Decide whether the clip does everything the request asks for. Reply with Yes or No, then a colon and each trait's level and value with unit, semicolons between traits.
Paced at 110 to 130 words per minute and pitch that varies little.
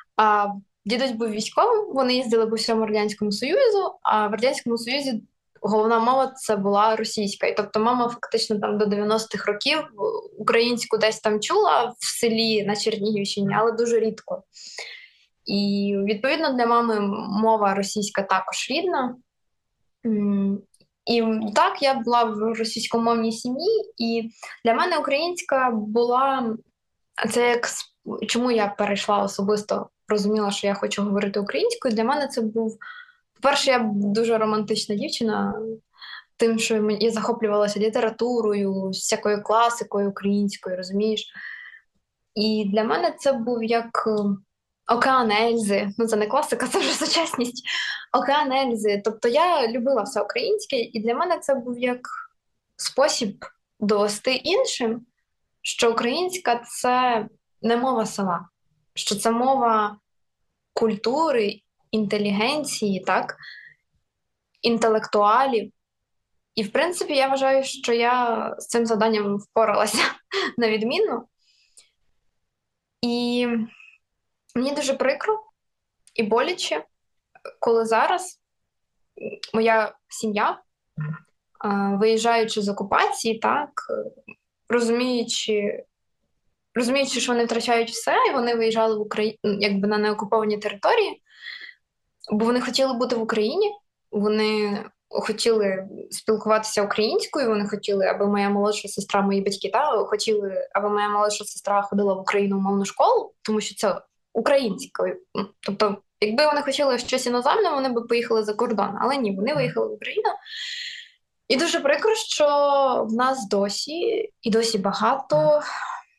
No: average, 120 wpm; average, 3.9 semitones